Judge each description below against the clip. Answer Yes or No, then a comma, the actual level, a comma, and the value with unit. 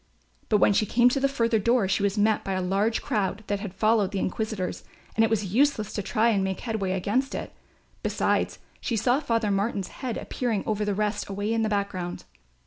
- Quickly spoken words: Yes, fast, 215 wpm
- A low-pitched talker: No, high, 210 Hz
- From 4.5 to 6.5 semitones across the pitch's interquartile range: No, narrow, 2.6 semitones